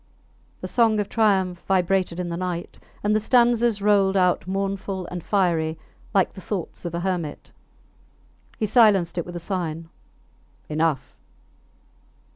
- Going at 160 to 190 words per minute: No, average, 140 wpm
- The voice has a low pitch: No, medium, 185 Hz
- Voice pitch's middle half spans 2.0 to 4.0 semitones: Yes, average, 3.0 semitones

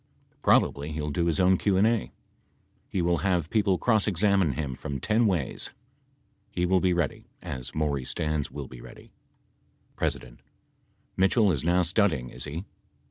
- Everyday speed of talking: Yes, average, 165 wpm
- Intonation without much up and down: No, average, 4.6 semitones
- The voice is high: No, very low, 85 Hz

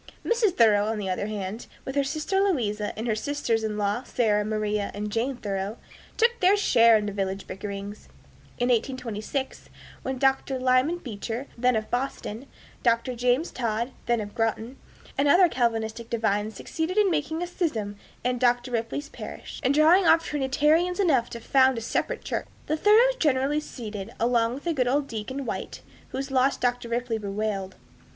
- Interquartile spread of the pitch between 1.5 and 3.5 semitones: No, average, 4.7 semitones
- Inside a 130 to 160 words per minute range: No, average, 170 wpm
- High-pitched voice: Yes, high, 245 Hz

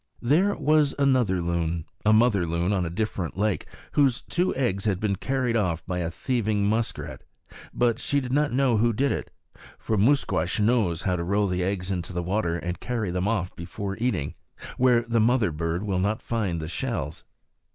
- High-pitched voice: No, low, 105 Hz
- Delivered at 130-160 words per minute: No, average, 185 wpm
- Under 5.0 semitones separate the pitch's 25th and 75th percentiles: No, wide, 5.4 semitones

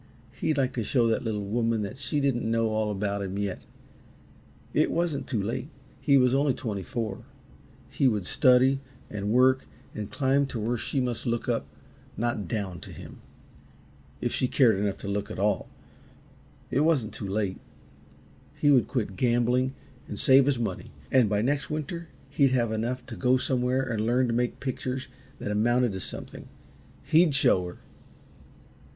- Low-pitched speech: Yes, low, 120 Hz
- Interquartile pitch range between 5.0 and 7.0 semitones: No, average, 3.8 semitones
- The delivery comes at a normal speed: Yes, average, 170 wpm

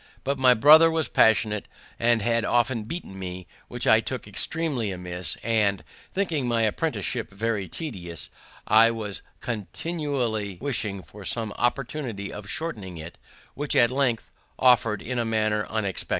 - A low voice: Yes, low, 115 Hz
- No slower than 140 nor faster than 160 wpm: Yes, average, 145 wpm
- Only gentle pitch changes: No, average, 4.4 semitones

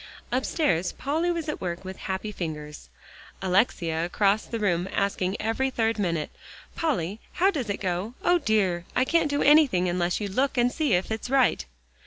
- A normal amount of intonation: No, wide, 6.8 semitones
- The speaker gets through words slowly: No, average, 175 wpm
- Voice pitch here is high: Yes, high, 205 Hz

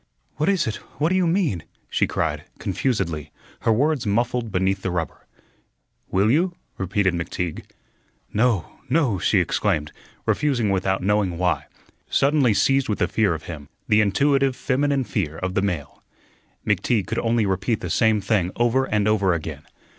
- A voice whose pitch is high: No, low, 105 Hz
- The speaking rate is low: No, average, 160 wpm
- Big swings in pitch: Yes, wide, 5.8 semitones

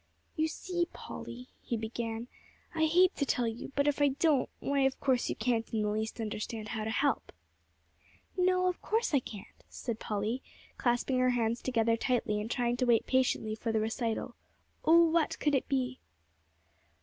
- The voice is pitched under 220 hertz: No, high, 245 Hz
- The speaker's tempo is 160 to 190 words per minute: Yes, average, 180 wpm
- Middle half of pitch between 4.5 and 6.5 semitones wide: No, average, 4.1 semitones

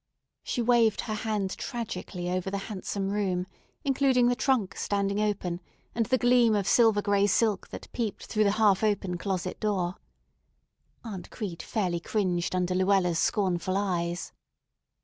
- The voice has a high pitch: Yes, high, 200 Hz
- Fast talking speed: No, average, 150 wpm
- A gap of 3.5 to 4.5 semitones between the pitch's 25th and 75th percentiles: No, average, 3.1 semitones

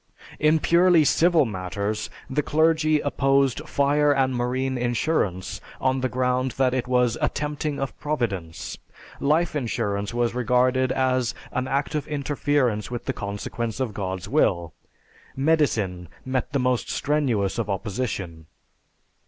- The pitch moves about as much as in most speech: Yes, average, 4.8 semitones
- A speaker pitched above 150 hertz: No, low, 130 Hz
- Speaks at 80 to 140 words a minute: Yes, slow, 135 wpm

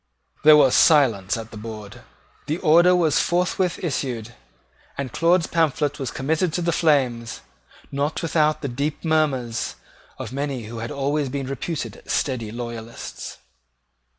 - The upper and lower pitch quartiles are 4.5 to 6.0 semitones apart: Yes, average, 5.0 semitones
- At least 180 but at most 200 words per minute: No, average, 140 wpm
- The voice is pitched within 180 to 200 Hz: No, medium, 140 Hz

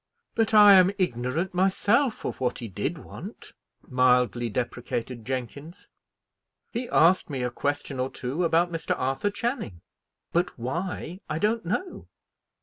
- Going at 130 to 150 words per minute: Yes, average, 140 wpm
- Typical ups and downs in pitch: No, wide, 7.4 semitones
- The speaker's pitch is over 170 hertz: No, medium, 160 Hz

